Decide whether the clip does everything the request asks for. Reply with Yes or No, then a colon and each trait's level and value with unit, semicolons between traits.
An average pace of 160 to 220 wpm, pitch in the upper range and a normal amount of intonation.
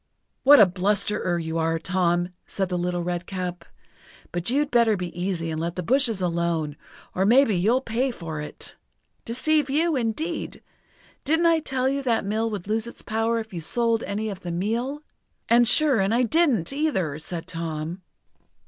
No: average, 175 wpm; high, 210 Hz; wide, 6.2 semitones